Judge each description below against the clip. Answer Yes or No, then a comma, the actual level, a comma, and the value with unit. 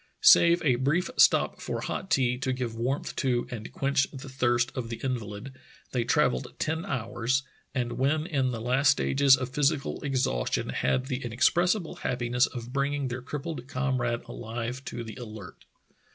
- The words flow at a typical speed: Yes, average, 165 wpm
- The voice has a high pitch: No, low, 130 Hz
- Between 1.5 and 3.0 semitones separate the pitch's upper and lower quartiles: Yes, narrow, 2.5 semitones